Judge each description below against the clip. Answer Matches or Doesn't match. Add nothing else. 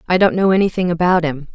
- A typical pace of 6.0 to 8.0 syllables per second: Matches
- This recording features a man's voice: Doesn't match